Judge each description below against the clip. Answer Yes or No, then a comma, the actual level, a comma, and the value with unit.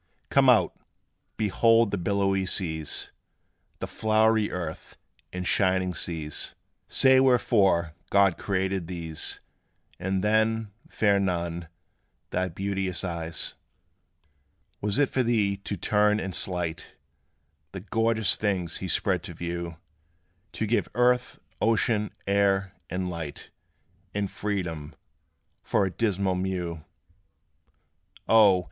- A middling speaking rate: No, slow, 110 wpm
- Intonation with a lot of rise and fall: No, average, 3.3 semitones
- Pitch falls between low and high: No, very low, 95 Hz